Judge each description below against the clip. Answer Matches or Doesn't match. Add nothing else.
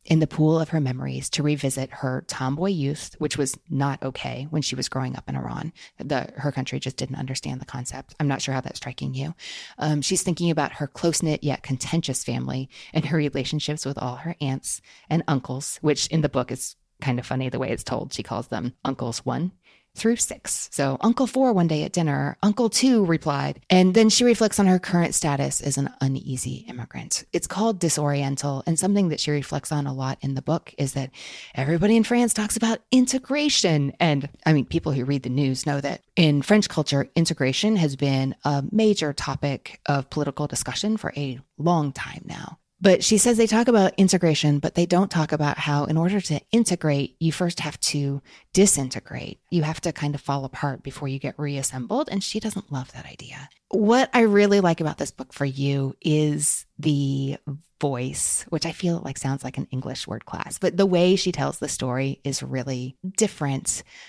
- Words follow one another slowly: Doesn't match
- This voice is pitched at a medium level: Matches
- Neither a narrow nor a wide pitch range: Matches